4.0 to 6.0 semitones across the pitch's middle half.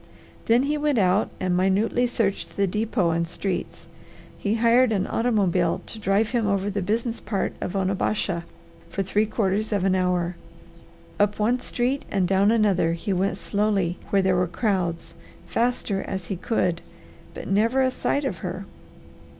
No: average, 3.4 semitones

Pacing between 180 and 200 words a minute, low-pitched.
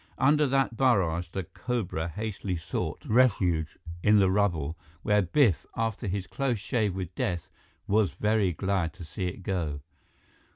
No: average, 150 wpm; very low, 95 Hz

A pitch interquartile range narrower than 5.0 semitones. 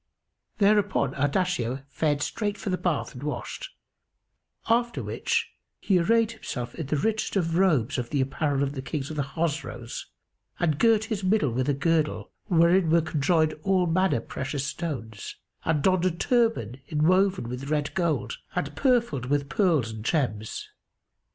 No: wide, 5.5 semitones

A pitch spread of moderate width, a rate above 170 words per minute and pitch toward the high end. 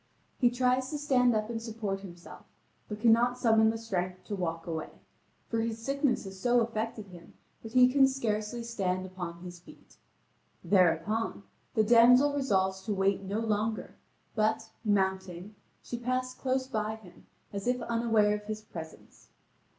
No: average, 3.9 semitones; average, 160 wpm; high, 220 Hz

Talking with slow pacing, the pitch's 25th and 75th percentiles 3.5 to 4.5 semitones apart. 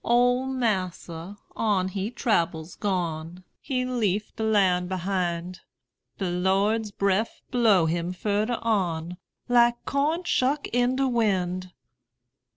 No: slow, 115 wpm; average, 4.9 semitones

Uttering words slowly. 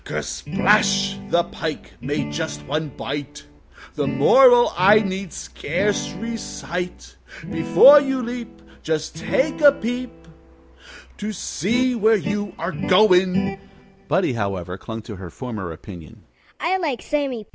Yes: slow, 115 wpm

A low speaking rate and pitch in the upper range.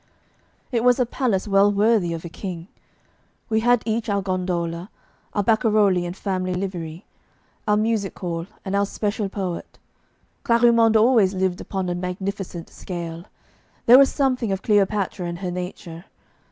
No: average, 150 wpm; high, 195 Hz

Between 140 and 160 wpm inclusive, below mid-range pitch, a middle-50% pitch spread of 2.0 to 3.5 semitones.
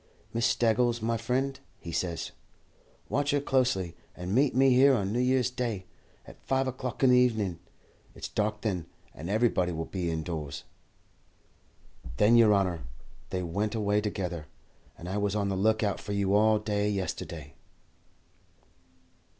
No: average, 155 wpm; low, 105 Hz; average, 4.9 semitones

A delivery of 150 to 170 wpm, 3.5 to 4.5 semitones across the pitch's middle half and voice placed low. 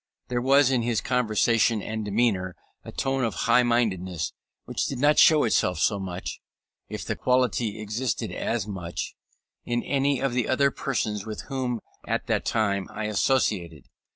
Yes: average, 160 wpm; average, 3.8 semitones; low, 115 Hz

